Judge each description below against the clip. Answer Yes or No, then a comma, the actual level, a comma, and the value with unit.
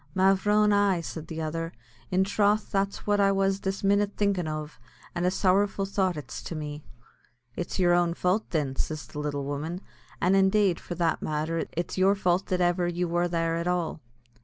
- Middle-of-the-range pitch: Yes, medium, 180 Hz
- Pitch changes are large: No, average, 2.9 semitones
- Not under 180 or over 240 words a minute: Yes, average, 190 wpm